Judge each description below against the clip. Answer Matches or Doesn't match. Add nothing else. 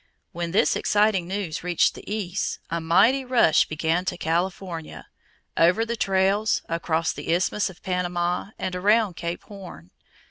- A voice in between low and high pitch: Matches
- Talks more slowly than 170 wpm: Matches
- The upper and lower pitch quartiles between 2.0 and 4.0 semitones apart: Matches